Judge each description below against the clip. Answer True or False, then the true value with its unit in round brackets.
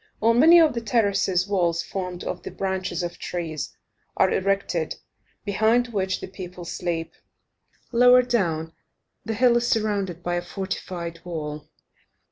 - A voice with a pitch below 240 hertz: True (190 Hz)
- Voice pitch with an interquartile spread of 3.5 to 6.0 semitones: True (4.4 semitones)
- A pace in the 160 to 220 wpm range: False (140 wpm)